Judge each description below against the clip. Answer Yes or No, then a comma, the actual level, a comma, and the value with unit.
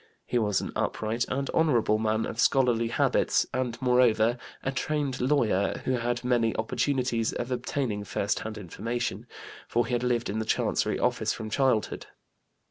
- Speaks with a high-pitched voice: No, low, 120 Hz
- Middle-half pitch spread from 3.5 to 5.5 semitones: No, narrow, 2.5 semitones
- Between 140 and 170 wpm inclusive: Yes, average, 160 wpm